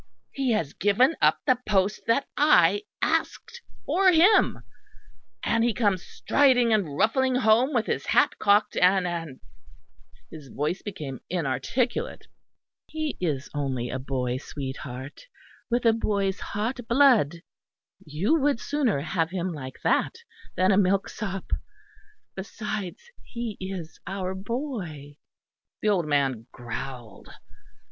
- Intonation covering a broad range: Yes, wide, 7.8 semitones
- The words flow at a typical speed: No, slow, 130 wpm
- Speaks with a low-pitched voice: No, high, 195 Hz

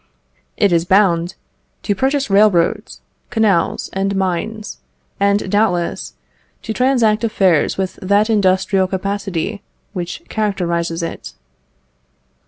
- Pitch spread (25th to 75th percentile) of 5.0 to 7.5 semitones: No, average, 3.0 semitones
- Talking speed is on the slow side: Yes, slow, 100 wpm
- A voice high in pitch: Yes, high, 195 Hz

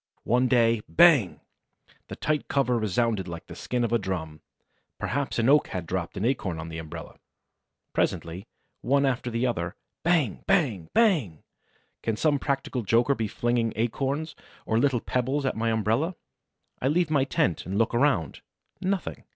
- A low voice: Yes, low, 120 Hz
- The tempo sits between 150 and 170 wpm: Yes, average, 160 wpm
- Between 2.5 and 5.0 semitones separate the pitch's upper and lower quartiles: No, wide, 5.6 semitones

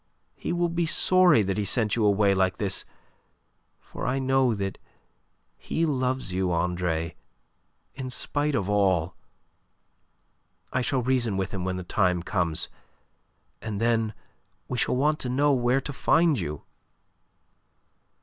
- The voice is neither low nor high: No, low, 110 Hz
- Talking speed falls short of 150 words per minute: Yes, average, 140 wpm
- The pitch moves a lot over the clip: Yes, wide, 6.0 semitones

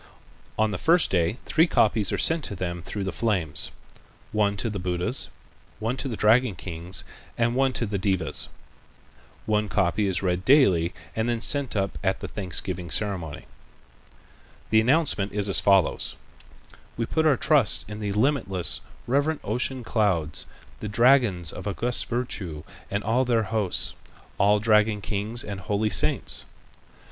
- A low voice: Yes, low, 105 Hz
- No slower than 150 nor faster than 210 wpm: Yes, average, 155 wpm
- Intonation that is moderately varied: Yes, average, 3.9 semitones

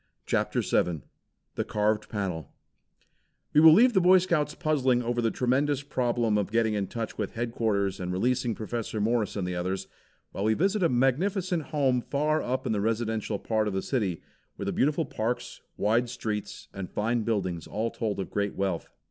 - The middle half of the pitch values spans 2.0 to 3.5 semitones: No, average, 4.3 semitones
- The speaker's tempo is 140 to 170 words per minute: No, average, 180 wpm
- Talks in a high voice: No, low, 115 Hz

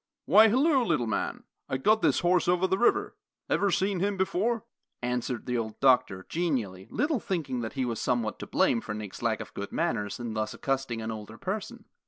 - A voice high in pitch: No, low, 135 Hz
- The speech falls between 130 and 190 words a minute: No, average, 200 wpm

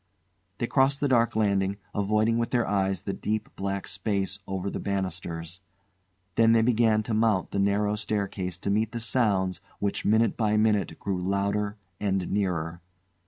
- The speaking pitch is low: Yes, low, 100 Hz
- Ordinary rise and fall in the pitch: No, narrow, 2.3 semitones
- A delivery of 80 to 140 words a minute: No, average, 165 wpm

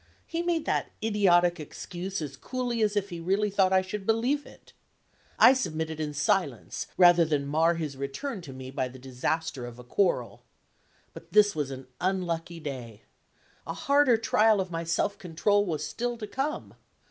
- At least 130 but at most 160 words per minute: No, average, 175 wpm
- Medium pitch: Yes, medium, 175 Hz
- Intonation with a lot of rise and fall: Yes, wide, 5.9 semitones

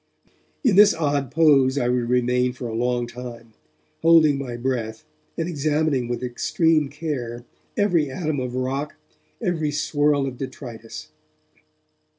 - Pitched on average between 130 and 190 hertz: Yes, low, 135 Hz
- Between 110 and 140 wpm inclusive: Yes, slow, 135 wpm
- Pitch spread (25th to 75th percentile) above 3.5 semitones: Yes, average, 3.9 semitones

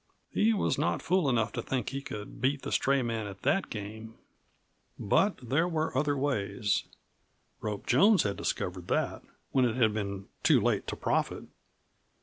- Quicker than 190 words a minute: No, average, 170 wpm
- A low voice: Yes, low, 120 Hz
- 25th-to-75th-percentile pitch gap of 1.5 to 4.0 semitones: No, wide, 5.4 semitones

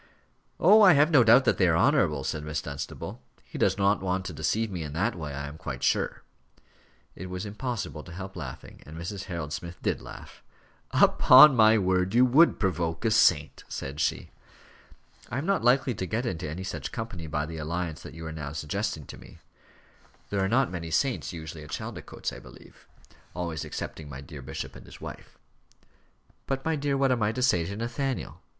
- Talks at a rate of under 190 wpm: No, average, 200 wpm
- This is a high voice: No, very low, 90 Hz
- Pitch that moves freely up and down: Yes, wide, 7.2 semitones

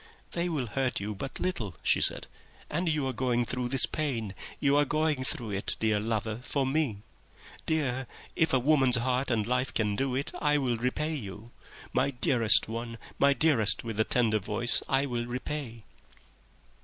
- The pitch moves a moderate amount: Yes, average, 3.8 semitones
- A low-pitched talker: Yes, low, 125 Hz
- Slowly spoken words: No, average, 180 wpm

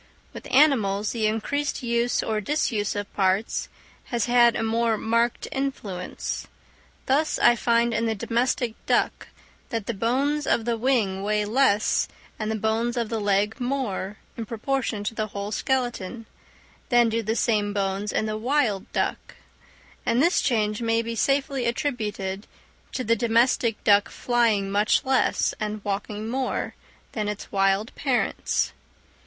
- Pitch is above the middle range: Yes, high, 225 Hz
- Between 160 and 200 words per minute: No, average, 150 wpm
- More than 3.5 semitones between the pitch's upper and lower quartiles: No, narrow, 2.6 semitones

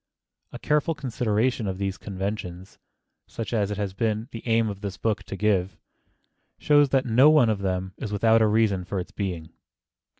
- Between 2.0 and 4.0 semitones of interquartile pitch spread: Yes, average, 3.0 semitones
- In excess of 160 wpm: Yes, average, 180 wpm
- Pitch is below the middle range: Yes, low, 105 Hz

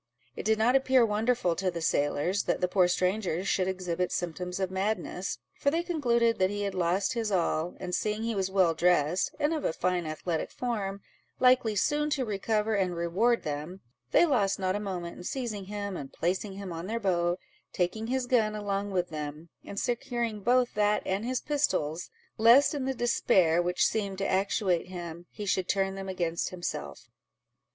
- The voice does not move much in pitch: No, average, 4.1 semitones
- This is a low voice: No, high, 195 Hz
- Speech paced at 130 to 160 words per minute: No, average, 190 wpm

